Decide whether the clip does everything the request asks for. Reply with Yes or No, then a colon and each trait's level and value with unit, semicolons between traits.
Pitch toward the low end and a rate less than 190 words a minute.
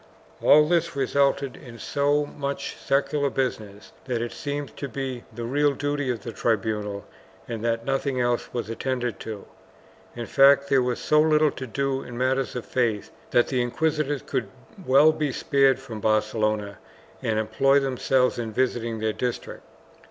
Yes: low, 130 Hz; average, 165 wpm